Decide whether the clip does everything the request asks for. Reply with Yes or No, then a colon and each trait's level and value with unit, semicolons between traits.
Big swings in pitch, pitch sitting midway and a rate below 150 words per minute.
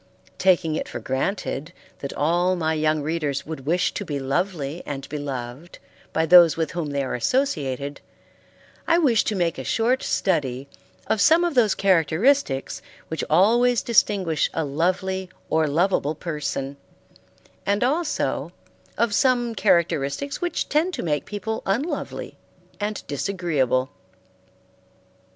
Yes: wide, 6.4 semitones; medium, 170 Hz; slow, 135 wpm